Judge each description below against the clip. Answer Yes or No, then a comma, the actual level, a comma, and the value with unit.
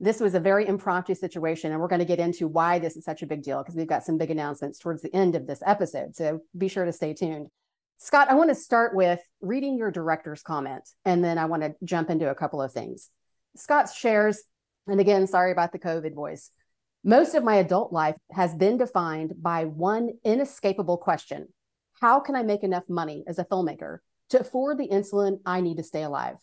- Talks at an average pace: No, fast, 220 wpm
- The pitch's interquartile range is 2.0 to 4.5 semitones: Yes, average, 3.9 semitones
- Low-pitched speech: No, medium, 180 Hz